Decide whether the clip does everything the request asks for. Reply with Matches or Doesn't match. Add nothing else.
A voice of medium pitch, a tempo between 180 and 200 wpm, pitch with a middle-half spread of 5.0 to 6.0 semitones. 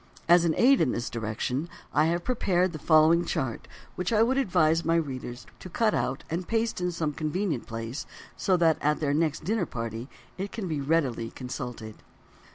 Matches